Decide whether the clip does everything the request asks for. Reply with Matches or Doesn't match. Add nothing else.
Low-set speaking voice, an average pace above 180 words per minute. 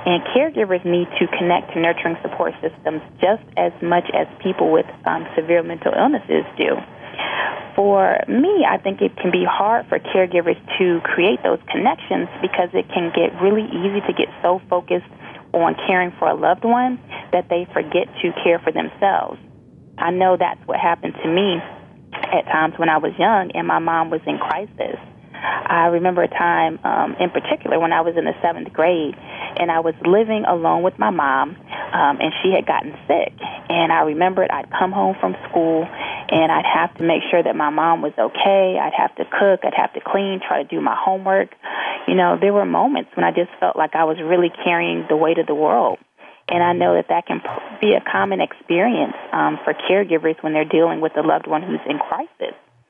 Doesn't match